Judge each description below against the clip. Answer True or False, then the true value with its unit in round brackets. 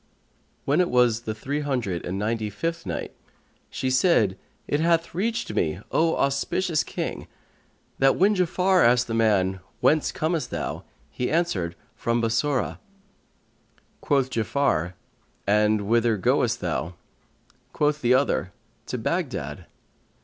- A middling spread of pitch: False (6.7 semitones)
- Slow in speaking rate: True (130 wpm)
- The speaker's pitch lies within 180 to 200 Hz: False (125 Hz)